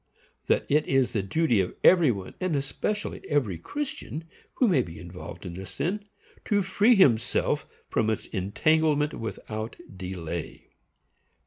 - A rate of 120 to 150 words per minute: Yes, average, 145 wpm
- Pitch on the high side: No, low, 135 Hz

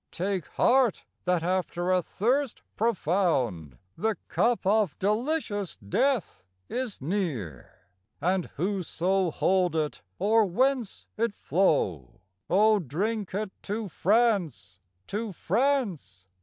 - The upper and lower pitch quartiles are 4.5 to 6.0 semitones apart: Yes, average, 5.0 semitones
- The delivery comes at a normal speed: No, slow, 105 wpm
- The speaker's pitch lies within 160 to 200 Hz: Yes, high, 190 Hz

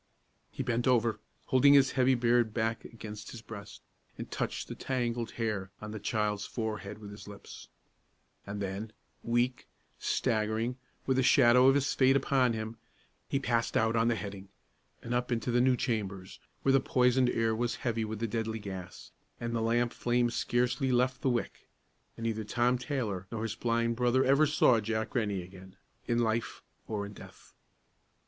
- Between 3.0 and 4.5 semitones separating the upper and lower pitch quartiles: No, narrow, 2.4 semitones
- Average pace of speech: Yes, average, 175 wpm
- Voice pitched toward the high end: No, low, 115 Hz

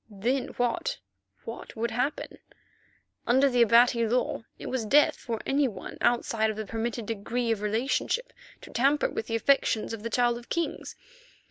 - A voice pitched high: Yes, high, 235 Hz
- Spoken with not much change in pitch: Yes, narrow, 2.3 semitones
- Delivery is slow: No, average, 160 wpm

